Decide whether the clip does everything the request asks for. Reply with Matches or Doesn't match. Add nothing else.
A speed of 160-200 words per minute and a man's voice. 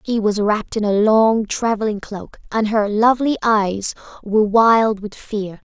Doesn't match